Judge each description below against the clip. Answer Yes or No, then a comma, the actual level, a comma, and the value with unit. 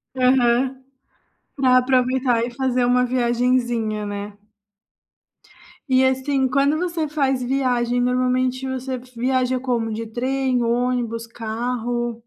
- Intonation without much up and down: Yes, narrow, 1.6 semitones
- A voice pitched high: Yes, very high, 250 Hz